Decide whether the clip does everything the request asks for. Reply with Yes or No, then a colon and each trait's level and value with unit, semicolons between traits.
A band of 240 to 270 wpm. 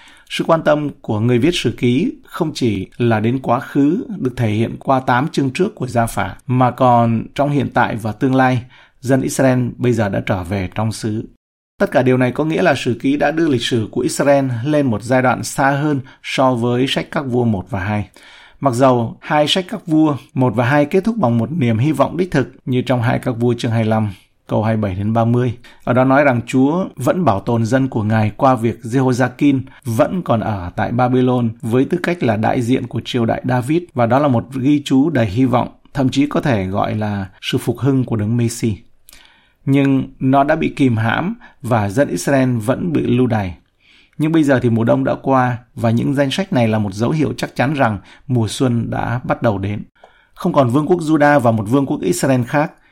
No: average, 225 wpm